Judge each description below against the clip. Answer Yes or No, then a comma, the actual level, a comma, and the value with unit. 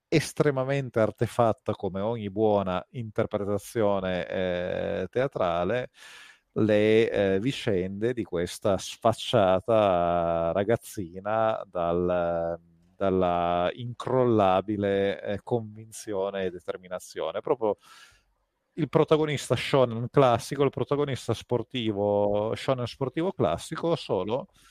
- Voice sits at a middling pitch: No, low, 110 Hz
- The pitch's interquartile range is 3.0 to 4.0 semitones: No, average, 4.6 semitones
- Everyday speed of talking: No, slow, 85 wpm